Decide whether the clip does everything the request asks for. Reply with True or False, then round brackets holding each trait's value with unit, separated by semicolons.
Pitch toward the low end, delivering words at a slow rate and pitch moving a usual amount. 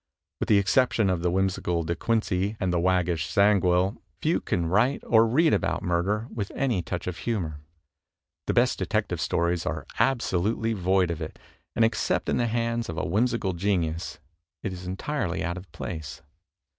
False (95 Hz; 175 wpm; 4.4 semitones)